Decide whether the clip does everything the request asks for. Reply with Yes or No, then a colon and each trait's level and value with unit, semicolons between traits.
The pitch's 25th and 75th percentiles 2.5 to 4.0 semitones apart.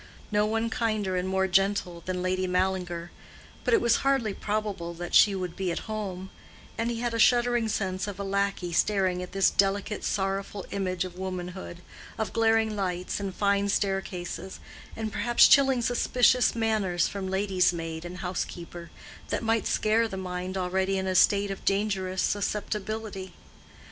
Yes: average, 2.8 semitones